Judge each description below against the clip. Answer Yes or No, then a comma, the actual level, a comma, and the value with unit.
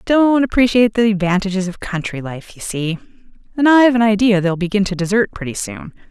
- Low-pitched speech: No, high, 205 Hz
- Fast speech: No, average, 185 wpm